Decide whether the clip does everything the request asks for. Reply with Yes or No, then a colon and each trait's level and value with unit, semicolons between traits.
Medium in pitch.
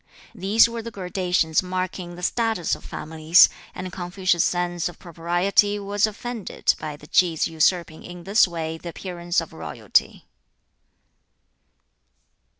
Yes: medium, 180 Hz